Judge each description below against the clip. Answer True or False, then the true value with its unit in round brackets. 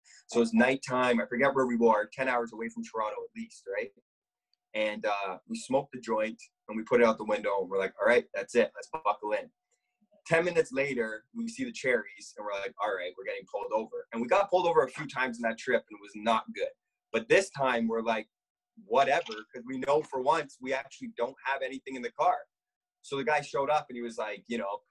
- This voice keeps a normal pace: False (245 wpm)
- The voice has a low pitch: False (150 Hz)